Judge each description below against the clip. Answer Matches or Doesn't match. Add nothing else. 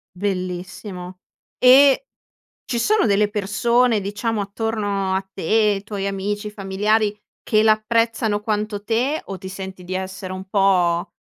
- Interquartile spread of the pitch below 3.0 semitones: Matches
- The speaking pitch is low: Doesn't match